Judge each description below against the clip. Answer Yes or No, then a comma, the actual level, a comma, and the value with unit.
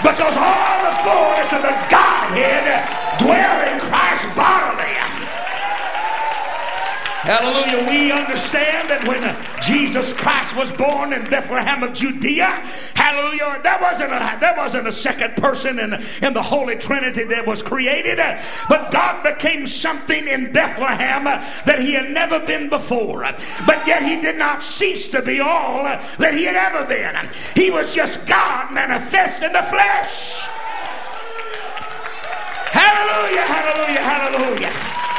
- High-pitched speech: Yes, very high, 285 Hz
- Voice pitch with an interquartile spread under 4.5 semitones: Yes, average, 3.9 semitones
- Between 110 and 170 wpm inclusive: Yes, slow, 135 wpm